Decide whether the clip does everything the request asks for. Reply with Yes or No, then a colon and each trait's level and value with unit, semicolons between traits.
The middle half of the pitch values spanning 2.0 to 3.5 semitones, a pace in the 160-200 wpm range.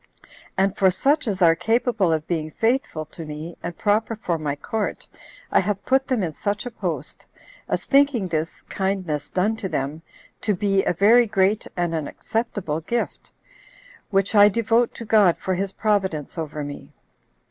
No: average, 5.2 semitones; average, 170 wpm